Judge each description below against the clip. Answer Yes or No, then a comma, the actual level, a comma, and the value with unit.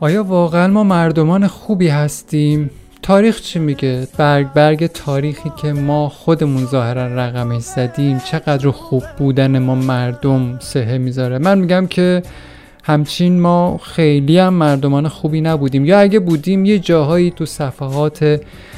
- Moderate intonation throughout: Yes, average, 4.2 semitones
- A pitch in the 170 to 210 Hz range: No, medium, 150 Hz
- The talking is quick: No, average, 135 wpm